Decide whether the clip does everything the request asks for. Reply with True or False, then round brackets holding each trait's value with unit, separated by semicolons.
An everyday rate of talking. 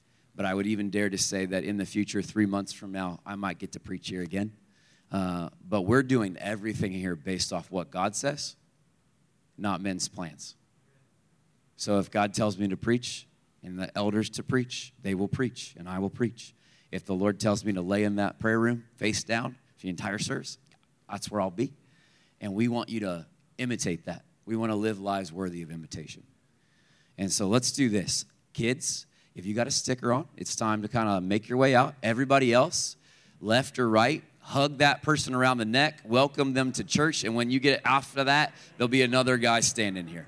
False (210 wpm)